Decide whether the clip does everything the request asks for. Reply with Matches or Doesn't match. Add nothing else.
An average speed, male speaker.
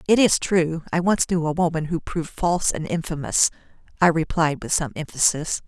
Doesn't match